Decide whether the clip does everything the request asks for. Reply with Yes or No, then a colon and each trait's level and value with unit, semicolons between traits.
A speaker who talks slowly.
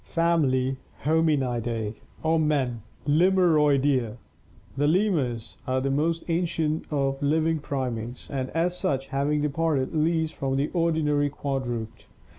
Yes: slow, 125 wpm